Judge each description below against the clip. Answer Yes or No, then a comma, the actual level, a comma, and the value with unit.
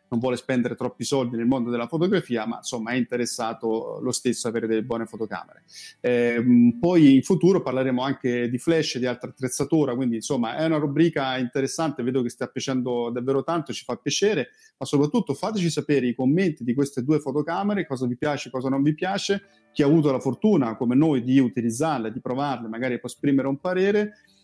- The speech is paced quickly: Yes, fast, 195 wpm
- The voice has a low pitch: Yes, low, 130 Hz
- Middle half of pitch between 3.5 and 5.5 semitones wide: Yes, average, 4.5 semitones